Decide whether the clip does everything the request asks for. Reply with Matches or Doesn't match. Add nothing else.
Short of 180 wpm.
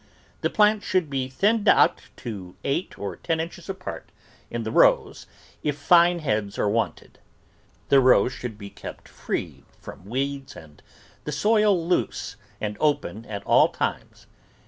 Matches